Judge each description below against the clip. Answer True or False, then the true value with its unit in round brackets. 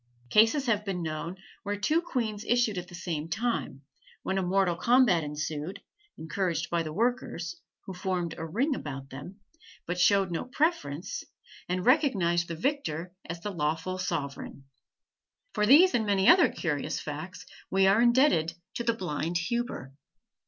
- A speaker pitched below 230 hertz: True (185 Hz)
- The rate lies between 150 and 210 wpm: True (155 wpm)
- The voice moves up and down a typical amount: False (5.8 semitones)